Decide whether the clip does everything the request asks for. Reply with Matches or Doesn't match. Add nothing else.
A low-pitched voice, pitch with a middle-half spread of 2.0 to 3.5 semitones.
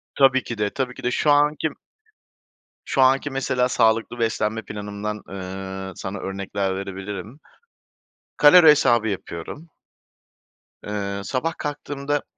Doesn't match